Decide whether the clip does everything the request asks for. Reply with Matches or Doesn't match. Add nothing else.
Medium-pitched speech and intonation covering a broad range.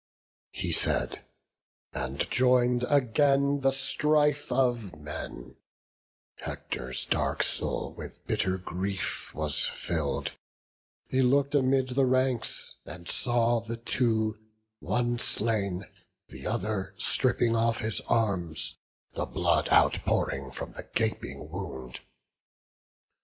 Doesn't match